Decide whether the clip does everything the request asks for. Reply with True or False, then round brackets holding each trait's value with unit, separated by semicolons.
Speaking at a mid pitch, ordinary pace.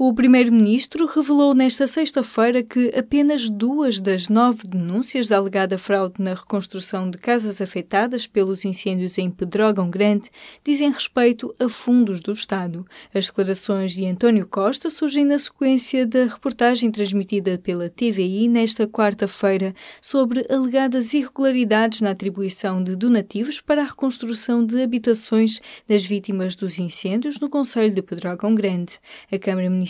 False (220 Hz; 130 wpm)